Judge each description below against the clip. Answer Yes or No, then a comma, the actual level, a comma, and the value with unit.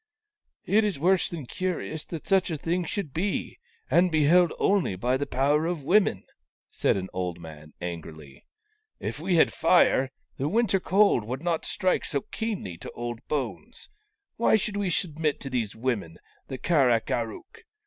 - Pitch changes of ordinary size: No, wide, 7.5 semitones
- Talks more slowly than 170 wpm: No, average, 180 wpm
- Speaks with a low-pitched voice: No, medium, 155 Hz